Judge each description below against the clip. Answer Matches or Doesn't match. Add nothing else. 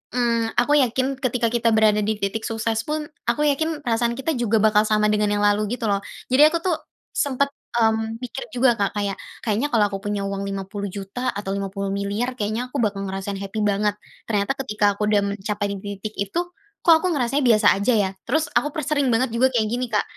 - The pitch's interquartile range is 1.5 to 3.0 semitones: Doesn't match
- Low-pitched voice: Doesn't match